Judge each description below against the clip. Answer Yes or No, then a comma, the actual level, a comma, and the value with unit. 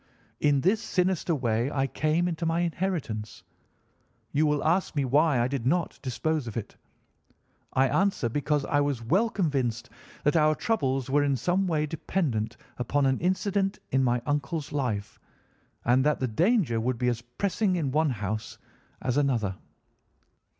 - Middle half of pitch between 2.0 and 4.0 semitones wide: No, wide, 5.5 semitones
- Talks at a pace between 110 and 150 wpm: No, average, 165 wpm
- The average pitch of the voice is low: No, medium, 145 Hz